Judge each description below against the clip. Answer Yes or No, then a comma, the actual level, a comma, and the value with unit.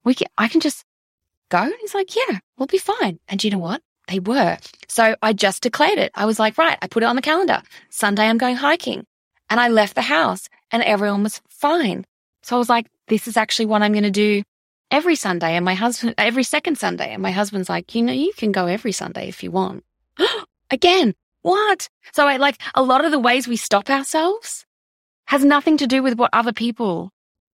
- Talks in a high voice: Yes, high, 240 Hz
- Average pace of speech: No, fast, 225 wpm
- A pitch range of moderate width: No, wide, 5.8 semitones